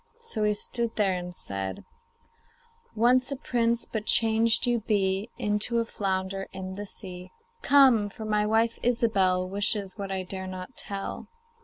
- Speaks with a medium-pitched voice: No, high, 210 Hz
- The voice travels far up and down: No, average, 3.4 semitones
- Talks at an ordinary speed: Yes, average, 155 wpm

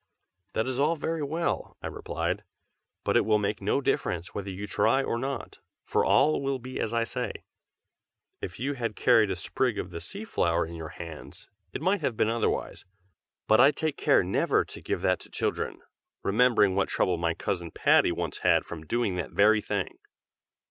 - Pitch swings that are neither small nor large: No, wide, 6.5 semitones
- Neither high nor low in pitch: No, low, 110 Hz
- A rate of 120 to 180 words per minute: No, average, 190 wpm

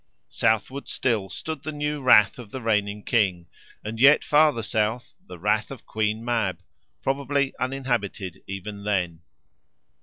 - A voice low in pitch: Yes, low, 110 Hz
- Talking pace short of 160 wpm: Yes, average, 140 wpm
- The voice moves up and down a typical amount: Yes, average, 4.9 semitones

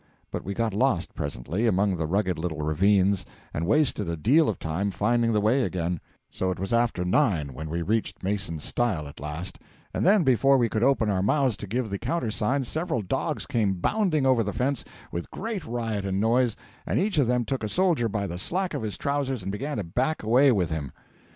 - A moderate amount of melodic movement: No, wide, 6.0 semitones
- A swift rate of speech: Yes, fast, 215 wpm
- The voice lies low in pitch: Yes, low, 110 Hz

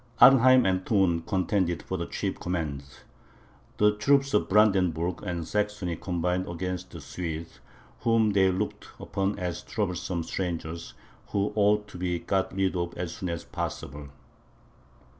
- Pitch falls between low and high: No, very low, 90 Hz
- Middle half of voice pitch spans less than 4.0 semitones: Yes, average, 3.2 semitones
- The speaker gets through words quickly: No, average, 140 wpm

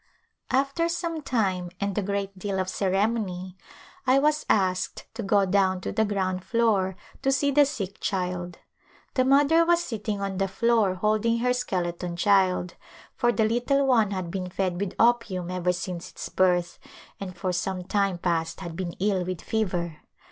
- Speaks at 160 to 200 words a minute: Yes, average, 175 wpm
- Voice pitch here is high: Yes, high, 195 Hz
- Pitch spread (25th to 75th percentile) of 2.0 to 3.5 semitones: No, average, 4.1 semitones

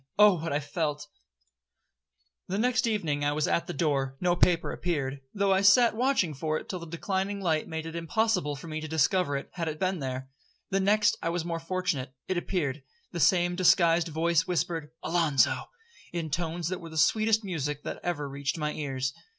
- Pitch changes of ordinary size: Yes, average, 3.8 semitones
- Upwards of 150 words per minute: Yes, average, 195 wpm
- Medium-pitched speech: Yes, medium, 165 Hz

